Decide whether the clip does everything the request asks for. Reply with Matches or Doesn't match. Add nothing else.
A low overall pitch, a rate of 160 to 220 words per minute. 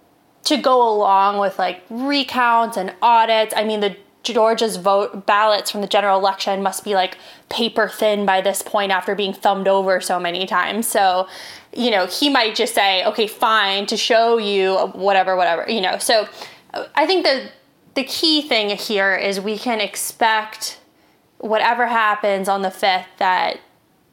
Doesn't match